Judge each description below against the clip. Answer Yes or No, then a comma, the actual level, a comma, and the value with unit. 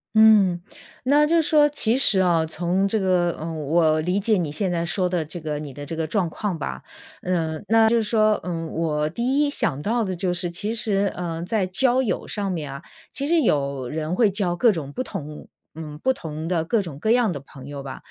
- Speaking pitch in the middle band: Yes, medium, 180 Hz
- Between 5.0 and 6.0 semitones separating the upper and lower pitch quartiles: Yes, wide, 5.5 semitones